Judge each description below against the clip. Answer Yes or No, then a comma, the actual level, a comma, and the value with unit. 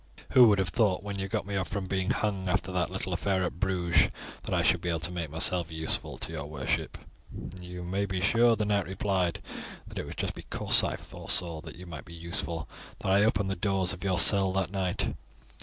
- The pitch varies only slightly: Yes, narrow, 2.2 semitones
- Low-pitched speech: Yes, very low, 95 Hz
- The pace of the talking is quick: Yes, fast, 225 wpm